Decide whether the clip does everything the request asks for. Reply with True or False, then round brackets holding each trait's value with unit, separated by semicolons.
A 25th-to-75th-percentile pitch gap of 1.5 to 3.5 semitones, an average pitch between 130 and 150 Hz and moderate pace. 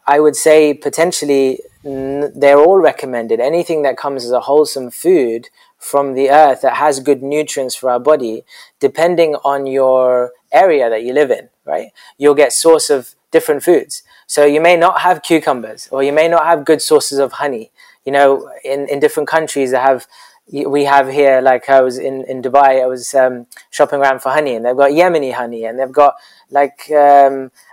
True (2.6 semitones; 140 Hz; 195 wpm)